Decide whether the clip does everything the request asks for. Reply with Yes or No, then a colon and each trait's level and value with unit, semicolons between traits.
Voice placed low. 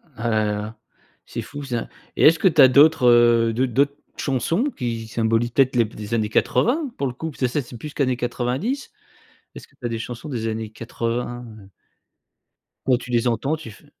Yes: low, 120 Hz